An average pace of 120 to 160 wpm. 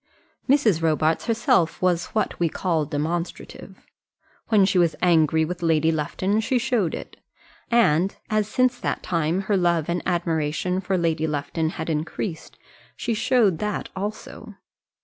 Yes: average, 145 wpm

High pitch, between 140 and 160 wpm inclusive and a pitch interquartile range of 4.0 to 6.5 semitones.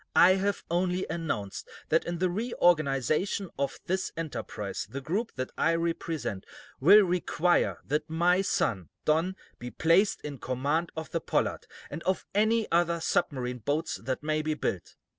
No: medium, 165 Hz; average, 155 wpm; average, 4.6 semitones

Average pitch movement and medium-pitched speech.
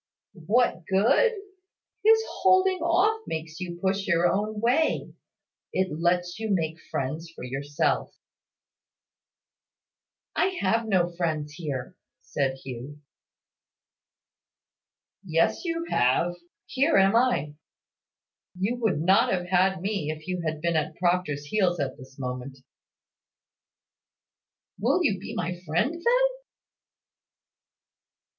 No: wide, 6.2 semitones; medium, 180 Hz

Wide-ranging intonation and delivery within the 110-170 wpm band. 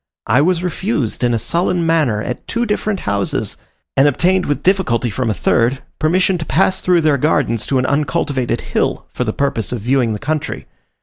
No: wide, 6.3 semitones; average, 190 wpm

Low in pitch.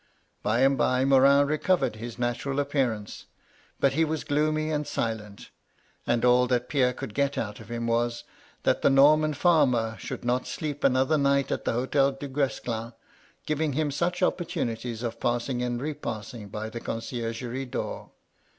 Yes: low, 130 Hz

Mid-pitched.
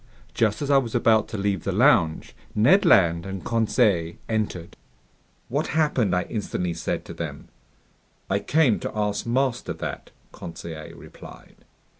No: low, 105 Hz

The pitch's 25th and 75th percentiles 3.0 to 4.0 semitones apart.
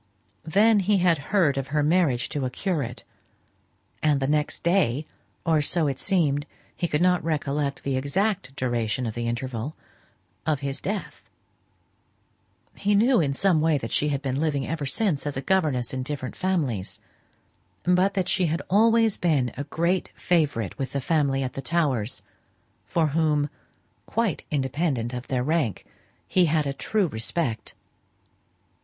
No: average, 4.7 semitones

